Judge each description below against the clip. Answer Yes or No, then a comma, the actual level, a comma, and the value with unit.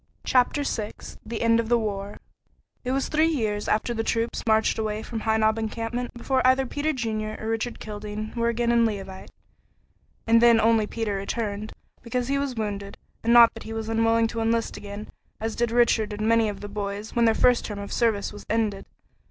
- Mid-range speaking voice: No, high, 225 Hz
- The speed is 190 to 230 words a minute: Yes, average, 200 wpm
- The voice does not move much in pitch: Yes, narrow, 1.8 semitones